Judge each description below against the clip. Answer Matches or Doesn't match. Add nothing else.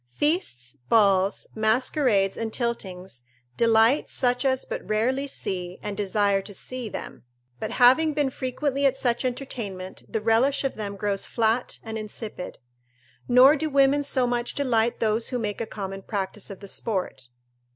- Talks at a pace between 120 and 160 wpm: Matches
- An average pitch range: Matches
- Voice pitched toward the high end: Matches